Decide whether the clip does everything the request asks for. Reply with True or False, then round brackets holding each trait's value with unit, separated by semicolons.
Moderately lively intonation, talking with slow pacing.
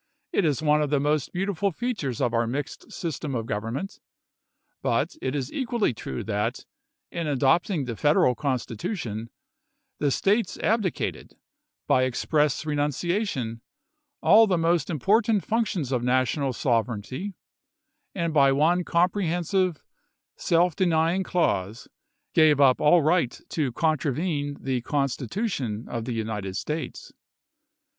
False (5.8 semitones; 130 wpm)